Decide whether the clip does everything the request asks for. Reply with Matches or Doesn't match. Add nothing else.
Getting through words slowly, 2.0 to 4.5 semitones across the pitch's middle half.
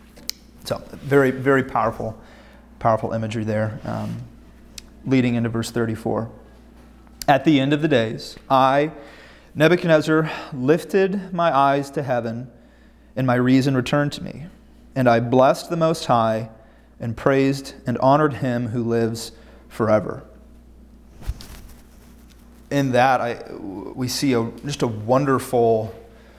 Matches